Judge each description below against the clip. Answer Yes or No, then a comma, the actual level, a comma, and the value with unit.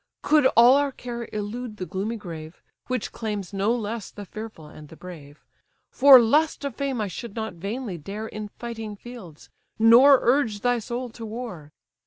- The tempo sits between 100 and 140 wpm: No, average, 175 wpm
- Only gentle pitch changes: No, average, 3.8 semitones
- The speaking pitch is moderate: No, high, 220 Hz